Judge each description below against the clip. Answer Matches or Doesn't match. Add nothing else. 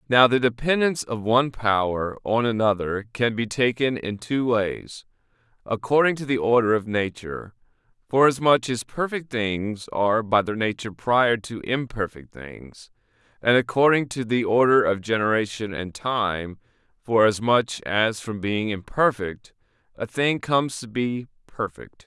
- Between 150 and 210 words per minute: Doesn't match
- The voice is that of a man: Matches